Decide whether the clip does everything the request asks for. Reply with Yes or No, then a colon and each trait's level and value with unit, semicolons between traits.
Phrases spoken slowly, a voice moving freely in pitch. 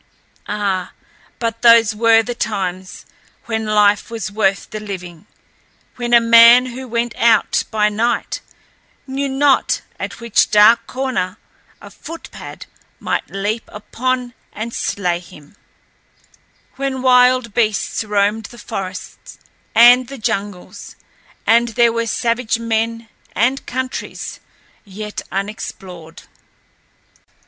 No: slow, 115 wpm; average, 2.7 semitones